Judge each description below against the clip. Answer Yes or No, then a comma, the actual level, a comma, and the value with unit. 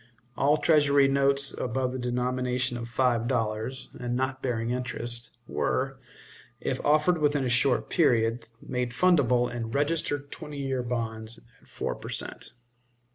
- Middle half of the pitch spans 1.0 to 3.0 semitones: Yes, narrow, 2.5 semitones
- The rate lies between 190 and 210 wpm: No, average, 140 wpm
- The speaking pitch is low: Yes, low, 125 Hz